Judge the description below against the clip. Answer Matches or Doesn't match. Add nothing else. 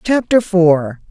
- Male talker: Doesn't match